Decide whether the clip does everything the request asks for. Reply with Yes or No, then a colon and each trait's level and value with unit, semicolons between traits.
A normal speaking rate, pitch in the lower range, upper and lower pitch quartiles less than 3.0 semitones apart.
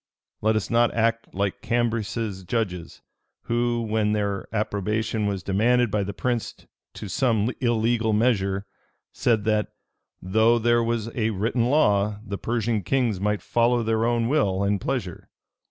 Yes: average, 145 wpm; low, 110 Hz; narrow, 2.5 semitones